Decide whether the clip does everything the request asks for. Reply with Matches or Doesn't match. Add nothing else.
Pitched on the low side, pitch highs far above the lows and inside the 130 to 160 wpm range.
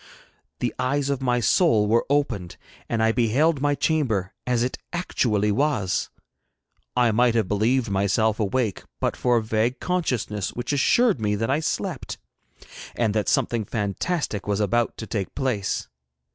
Doesn't match